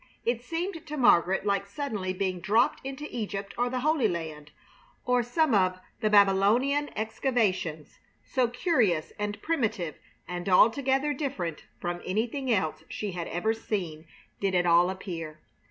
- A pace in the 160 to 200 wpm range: No, average, 145 wpm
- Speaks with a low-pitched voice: No, high, 210 Hz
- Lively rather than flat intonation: Yes, wide, 5.7 semitones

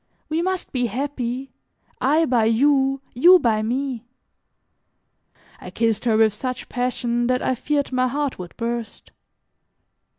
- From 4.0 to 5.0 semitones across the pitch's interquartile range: No, average, 3.0 semitones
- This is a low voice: No, very high, 250 Hz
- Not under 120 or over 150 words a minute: Yes, slow, 135 wpm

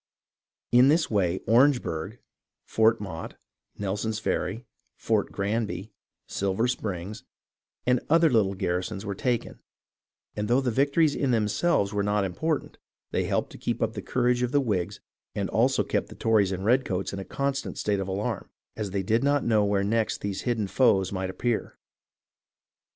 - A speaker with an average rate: Yes, average, 165 wpm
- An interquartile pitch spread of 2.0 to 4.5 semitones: Yes, average, 4.1 semitones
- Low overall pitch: Yes, low, 110 Hz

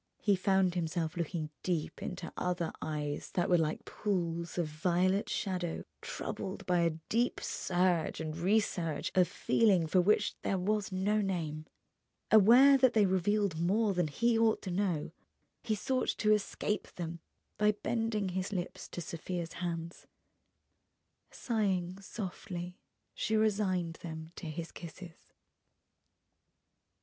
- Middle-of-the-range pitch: Yes, medium, 180 Hz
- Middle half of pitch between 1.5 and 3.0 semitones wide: No, average, 3.5 semitones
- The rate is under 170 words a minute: Yes, slow, 135 wpm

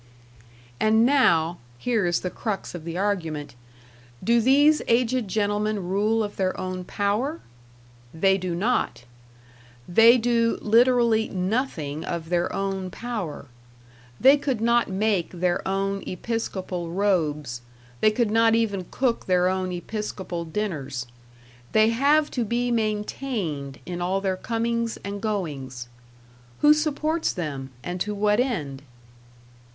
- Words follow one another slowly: Yes, slow, 130 wpm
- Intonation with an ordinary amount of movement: Yes, average, 4.7 semitones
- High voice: Yes, high, 205 Hz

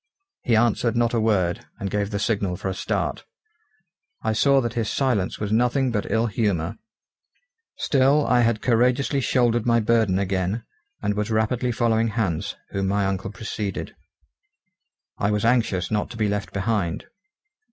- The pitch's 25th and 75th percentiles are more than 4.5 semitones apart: No, average, 2.9 semitones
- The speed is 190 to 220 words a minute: No, average, 160 wpm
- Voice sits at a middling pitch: No, low, 110 Hz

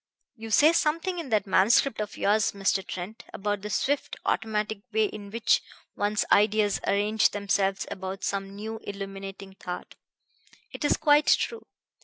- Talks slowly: No, average, 150 wpm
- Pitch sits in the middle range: No, high, 210 Hz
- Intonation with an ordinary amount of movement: No, narrow, 2.2 semitones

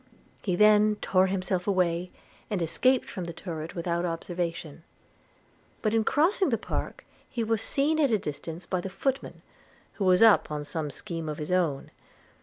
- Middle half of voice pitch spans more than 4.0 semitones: Yes, average, 4.4 semitones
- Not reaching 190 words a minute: Yes, average, 170 wpm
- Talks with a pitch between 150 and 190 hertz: Yes, medium, 185 Hz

